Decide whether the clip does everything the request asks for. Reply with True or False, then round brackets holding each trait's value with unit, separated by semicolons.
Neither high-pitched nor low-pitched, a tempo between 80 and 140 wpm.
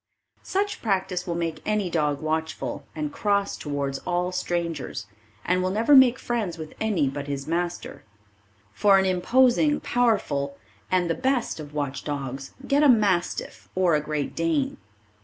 False (175 Hz; 155 wpm)